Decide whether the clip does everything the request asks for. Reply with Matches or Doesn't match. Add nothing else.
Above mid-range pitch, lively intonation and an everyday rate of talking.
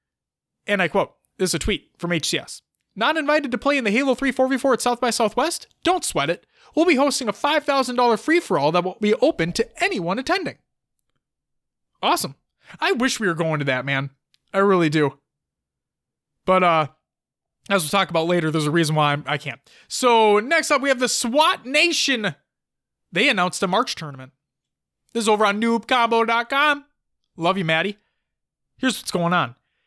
Matches